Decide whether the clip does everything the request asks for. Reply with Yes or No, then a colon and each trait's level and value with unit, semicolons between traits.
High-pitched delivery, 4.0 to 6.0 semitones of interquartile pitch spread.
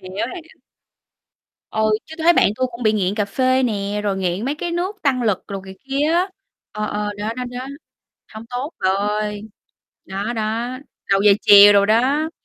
Yes: high, 220 Hz; average, 4.4 semitones